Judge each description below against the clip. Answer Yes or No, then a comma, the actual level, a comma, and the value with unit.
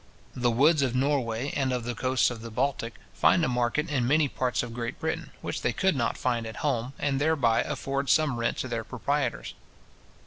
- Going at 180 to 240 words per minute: Yes, fast, 205 wpm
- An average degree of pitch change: Yes, average, 3.1 semitones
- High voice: No, low, 125 Hz